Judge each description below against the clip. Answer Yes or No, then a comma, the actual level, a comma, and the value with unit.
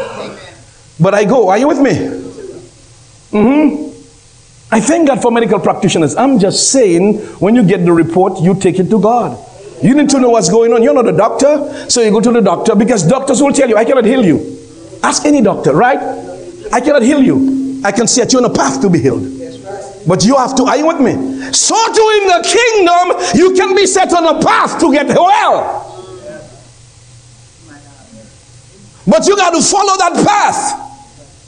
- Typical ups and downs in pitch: No, wide, 8.0 semitones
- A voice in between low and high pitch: No, high, 240 Hz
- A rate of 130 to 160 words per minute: No, average, 195 wpm